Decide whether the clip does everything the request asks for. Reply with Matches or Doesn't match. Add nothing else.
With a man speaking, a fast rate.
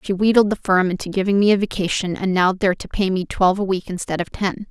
Doesn't match